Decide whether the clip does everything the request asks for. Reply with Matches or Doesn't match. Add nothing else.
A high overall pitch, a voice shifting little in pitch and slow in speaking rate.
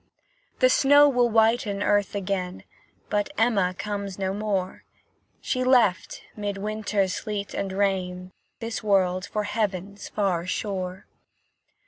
Matches